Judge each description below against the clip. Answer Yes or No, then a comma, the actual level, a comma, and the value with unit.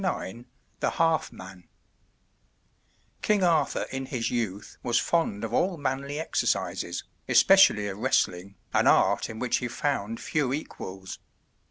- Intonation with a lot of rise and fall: Yes, wide, 6.4 semitones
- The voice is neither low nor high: No, low, 125 Hz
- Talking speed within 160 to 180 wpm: No, slow, 135 wpm